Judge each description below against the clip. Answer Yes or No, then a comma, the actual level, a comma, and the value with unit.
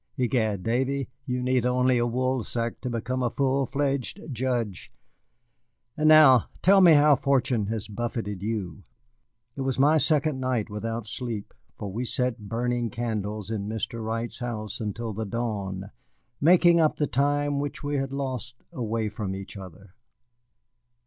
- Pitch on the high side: No, low, 120 Hz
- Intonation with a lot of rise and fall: No, average, 3.7 semitones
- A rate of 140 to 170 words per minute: Yes, average, 150 wpm